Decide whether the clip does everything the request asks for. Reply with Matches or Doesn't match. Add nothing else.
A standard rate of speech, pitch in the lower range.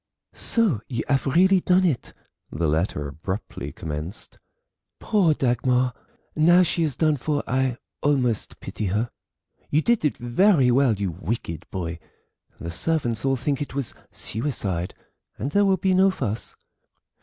Matches